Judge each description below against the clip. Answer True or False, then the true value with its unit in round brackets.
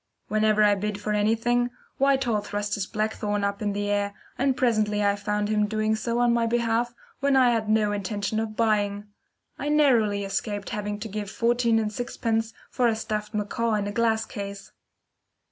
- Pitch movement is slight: True (2.1 semitones)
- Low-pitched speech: False (215 Hz)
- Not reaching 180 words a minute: False (185 wpm)